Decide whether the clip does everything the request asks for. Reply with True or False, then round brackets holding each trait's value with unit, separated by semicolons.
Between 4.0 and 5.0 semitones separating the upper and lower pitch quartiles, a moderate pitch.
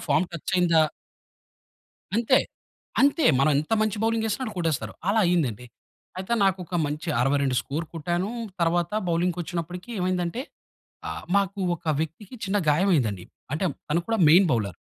True (4.4 semitones; 175 Hz)